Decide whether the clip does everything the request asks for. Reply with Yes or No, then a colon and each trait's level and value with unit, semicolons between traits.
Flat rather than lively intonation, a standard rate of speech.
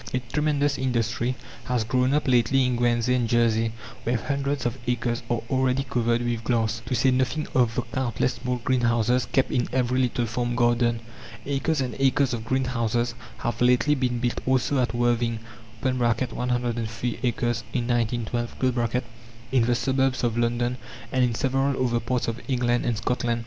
Yes: narrow, 1.6 semitones; average, 165 wpm